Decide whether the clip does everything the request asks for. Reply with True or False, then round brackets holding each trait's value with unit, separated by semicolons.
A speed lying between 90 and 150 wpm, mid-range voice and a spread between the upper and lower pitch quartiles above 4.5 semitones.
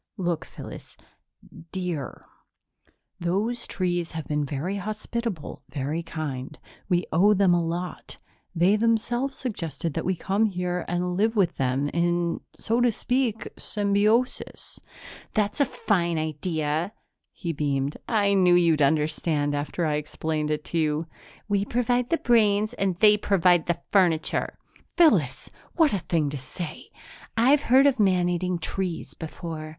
True (145 wpm; 180 Hz; 4.9 semitones)